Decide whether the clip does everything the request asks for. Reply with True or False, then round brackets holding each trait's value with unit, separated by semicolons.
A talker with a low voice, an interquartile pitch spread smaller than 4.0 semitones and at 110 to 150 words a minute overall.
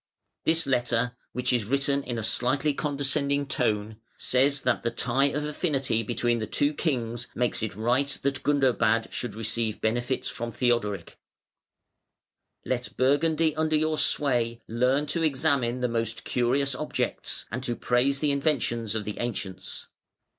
True (125 Hz; 3.3 semitones; 145 wpm)